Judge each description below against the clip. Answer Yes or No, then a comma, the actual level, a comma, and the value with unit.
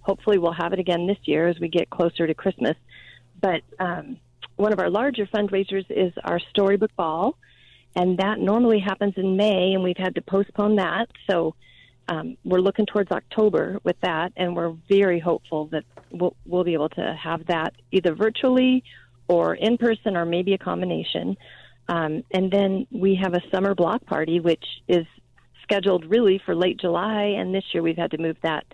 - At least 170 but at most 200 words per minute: Yes, average, 185 wpm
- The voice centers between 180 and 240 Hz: Yes, medium, 185 Hz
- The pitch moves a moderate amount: Yes, average, 3.3 semitones